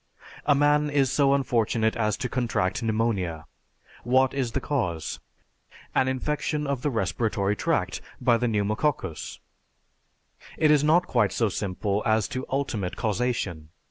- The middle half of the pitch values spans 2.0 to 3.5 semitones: No, average, 4.8 semitones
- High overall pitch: No, low, 120 Hz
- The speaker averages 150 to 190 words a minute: No, average, 140 wpm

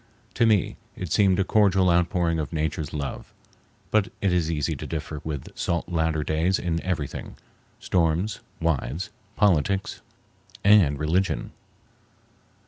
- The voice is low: Yes, very low, 85 Hz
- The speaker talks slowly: Yes, slow, 125 wpm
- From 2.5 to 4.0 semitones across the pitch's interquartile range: Yes, average, 3.4 semitones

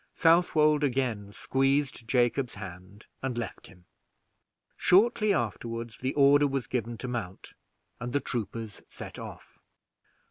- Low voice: Yes, low, 125 Hz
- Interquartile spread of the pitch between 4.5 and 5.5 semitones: No, average, 4.1 semitones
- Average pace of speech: No, slow, 120 wpm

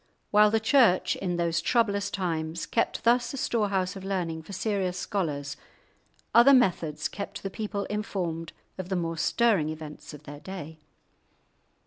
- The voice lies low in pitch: No, medium, 185 Hz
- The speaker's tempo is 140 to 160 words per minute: Yes, average, 150 wpm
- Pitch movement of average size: Yes, average, 4.4 semitones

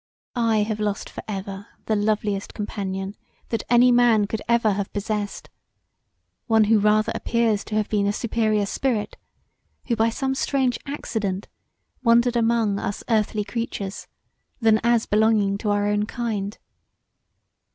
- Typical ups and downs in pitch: No, narrow, 2.2 semitones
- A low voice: No, high, 215 Hz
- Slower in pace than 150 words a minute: Yes, average, 140 wpm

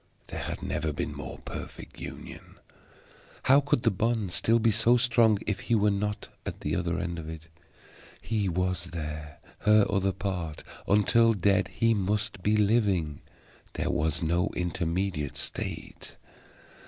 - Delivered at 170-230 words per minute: No, average, 150 wpm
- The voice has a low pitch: Yes, very low, 95 Hz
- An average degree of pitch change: Yes, average, 4.1 semitones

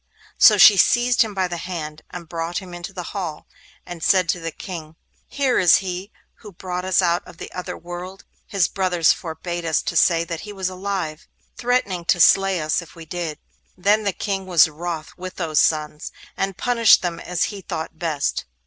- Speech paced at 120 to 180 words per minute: No, average, 195 wpm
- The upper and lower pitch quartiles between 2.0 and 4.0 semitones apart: Yes, narrow, 2.6 semitones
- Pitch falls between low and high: Yes, medium, 180 Hz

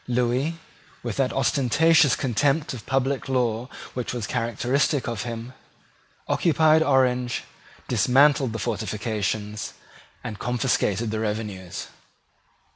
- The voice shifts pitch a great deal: No, average, 3.6 semitones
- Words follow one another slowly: Yes, slow, 105 wpm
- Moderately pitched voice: No, low, 125 Hz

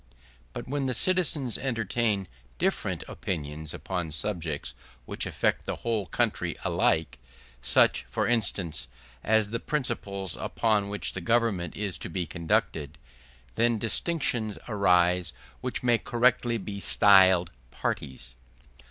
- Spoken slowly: Yes, slow, 120 wpm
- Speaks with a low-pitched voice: Yes, low, 100 Hz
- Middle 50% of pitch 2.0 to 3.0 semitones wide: No, average, 5.1 semitones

